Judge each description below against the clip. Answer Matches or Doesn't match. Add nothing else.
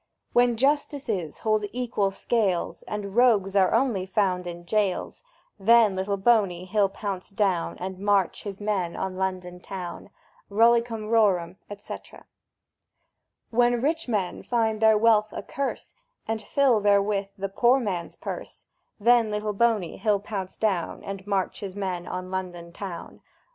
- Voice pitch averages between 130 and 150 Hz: Doesn't match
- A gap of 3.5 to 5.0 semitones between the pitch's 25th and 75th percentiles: Doesn't match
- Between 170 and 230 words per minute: Doesn't match